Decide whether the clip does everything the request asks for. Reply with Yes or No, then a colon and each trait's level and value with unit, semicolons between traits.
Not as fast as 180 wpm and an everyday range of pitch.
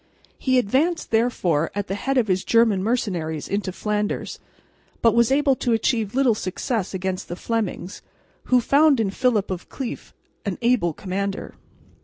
Yes: average, 155 wpm; average, 4.7 semitones